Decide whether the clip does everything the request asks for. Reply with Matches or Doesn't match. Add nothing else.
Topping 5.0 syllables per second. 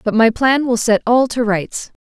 Doesn't match